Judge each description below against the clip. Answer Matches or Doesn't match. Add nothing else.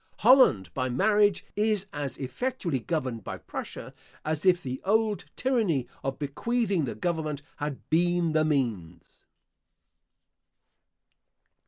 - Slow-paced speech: Matches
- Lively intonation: Matches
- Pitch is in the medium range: Matches